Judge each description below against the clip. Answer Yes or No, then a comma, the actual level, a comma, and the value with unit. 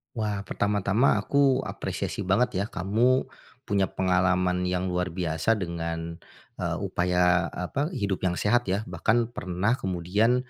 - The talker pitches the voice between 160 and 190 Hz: No, very low, 95 Hz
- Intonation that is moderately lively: Yes, average, 3.9 semitones